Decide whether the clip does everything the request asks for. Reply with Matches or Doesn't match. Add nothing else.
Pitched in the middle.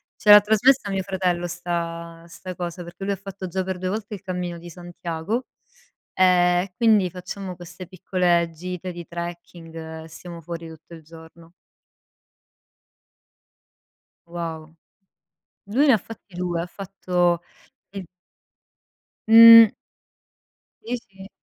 Matches